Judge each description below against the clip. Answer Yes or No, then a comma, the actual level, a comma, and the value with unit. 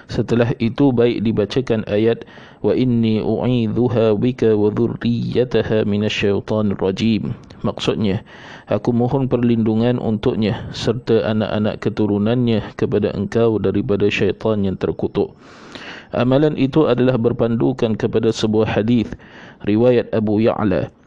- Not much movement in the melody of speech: Yes, narrow, 2.0 semitones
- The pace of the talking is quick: No, average, 105 wpm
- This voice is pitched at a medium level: No, low, 115 Hz